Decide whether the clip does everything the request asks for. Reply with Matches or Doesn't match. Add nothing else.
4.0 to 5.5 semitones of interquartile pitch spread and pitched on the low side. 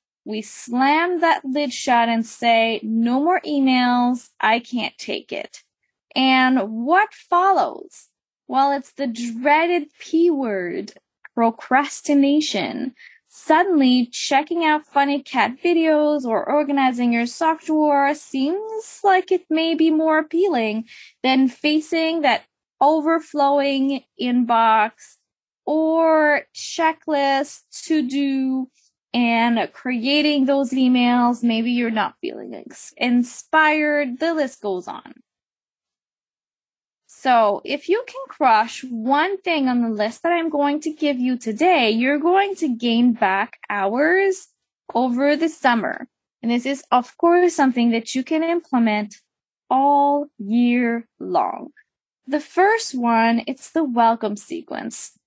Doesn't match